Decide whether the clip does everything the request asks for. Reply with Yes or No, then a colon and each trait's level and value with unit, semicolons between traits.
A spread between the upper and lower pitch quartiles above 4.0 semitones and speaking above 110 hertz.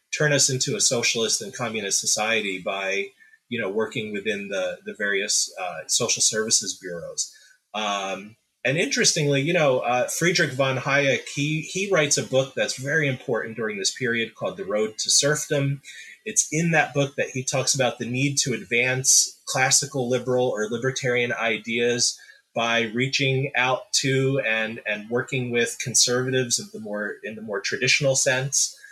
No: average, 3.4 semitones; low, 135 Hz